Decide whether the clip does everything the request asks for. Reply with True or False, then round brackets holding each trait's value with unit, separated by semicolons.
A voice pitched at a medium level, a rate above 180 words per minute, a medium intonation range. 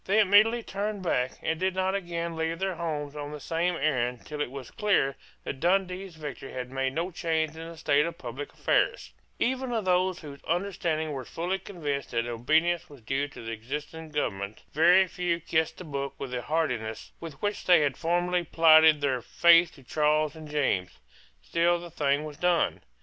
True (160 Hz; 190 wpm; 4.0 semitones)